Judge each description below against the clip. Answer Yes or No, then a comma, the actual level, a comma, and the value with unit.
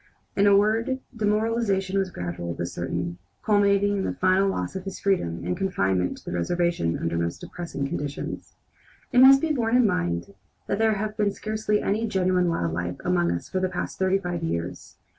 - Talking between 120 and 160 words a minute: No, average, 190 wpm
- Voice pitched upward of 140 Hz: Yes, medium, 185 Hz